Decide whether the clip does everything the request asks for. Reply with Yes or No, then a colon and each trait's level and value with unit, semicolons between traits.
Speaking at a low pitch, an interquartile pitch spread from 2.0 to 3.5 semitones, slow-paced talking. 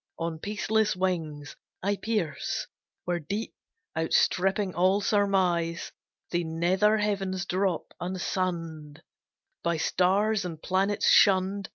No: medium, 185 Hz; average, 3.0 semitones; slow, 100 wpm